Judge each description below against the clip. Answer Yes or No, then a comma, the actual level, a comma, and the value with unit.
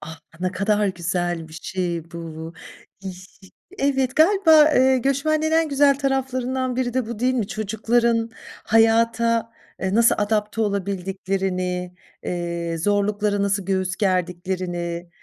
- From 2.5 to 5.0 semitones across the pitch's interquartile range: No, wide, 5.5 semitones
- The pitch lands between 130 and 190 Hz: No, high, 205 Hz